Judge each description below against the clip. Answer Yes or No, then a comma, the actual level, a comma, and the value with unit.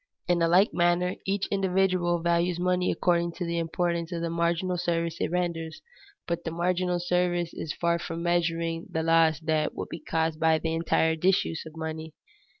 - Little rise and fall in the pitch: Yes, narrow, 1.4 semitones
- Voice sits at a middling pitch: Yes, medium, 170 Hz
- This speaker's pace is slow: No, average, 180 wpm